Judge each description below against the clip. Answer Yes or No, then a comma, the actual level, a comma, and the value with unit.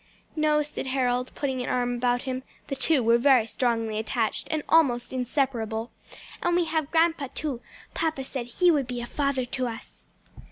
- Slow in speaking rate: No, average, 175 wpm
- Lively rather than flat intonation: No, average, 3.6 semitones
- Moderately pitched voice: No, very high, 260 Hz